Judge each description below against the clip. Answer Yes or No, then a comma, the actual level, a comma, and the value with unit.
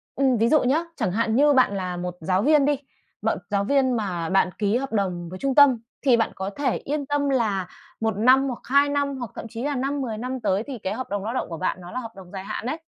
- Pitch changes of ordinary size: No, wide, 5.7 semitones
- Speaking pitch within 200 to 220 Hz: No, high, 235 Hz